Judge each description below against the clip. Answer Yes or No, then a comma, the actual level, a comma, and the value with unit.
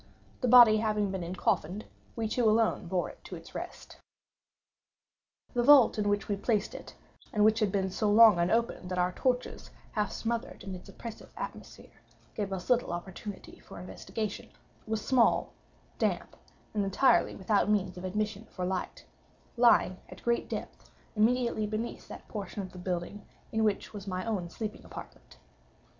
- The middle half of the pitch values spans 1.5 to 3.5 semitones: Yes, average, 3.1 semitones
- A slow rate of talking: No, average, 165 wpm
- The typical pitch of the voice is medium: No, high, 210 Hz